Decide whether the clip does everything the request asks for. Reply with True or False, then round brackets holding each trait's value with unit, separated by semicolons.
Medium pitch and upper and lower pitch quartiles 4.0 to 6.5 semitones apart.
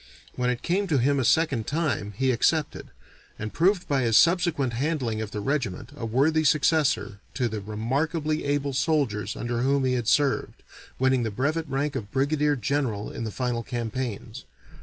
False (130 Hz; 4.6 semitones)